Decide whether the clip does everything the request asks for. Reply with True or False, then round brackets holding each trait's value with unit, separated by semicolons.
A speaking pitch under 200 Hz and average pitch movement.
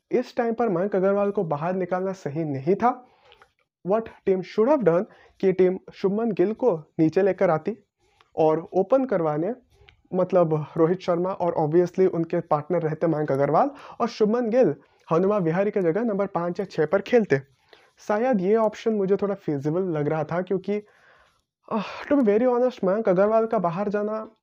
True (190 Hz; 4.2 semitones)